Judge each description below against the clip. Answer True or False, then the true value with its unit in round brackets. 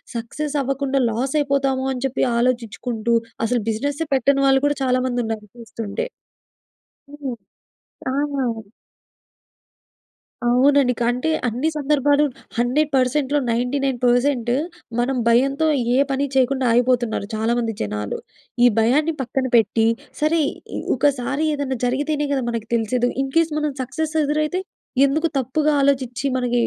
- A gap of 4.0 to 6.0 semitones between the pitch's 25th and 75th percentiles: False (2.9 semitones)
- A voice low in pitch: False (260 Hz)